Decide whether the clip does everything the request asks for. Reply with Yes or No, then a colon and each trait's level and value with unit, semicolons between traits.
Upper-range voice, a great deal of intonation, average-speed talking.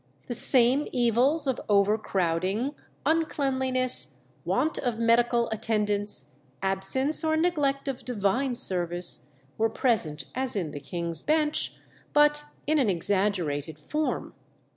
No: high, 235 Hz; wide, 6.1 semitones; slow, 115 wpm